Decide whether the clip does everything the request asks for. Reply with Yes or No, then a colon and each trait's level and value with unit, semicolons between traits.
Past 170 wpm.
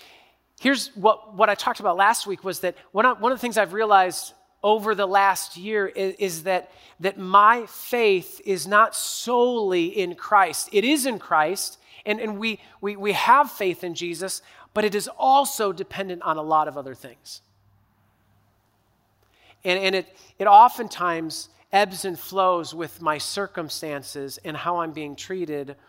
No: average, 165 wpm